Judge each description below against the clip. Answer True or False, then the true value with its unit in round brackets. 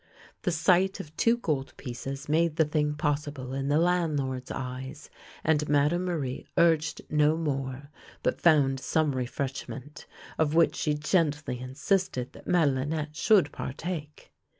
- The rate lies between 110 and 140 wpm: True (135 wpm)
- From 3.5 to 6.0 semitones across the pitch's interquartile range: False (3.1 semitones)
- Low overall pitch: False (150 Hz)